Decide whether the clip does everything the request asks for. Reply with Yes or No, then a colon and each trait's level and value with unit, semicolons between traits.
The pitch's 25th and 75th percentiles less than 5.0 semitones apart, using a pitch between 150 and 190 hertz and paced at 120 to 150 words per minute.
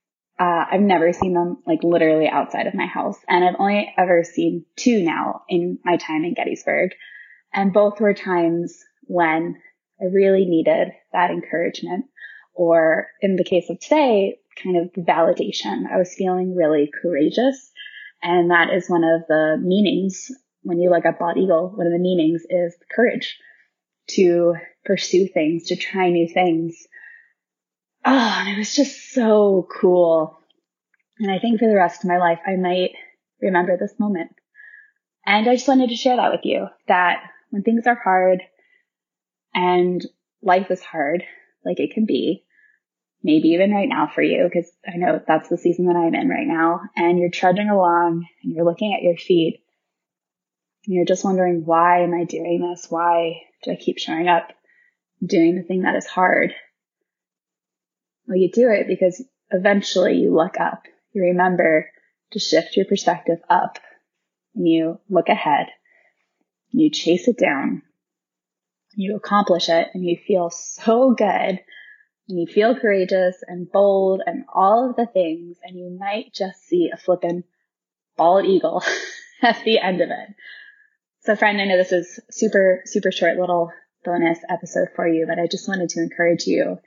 No: average, 3.7 semitones; medium, 185 Hz; average, 170 wpm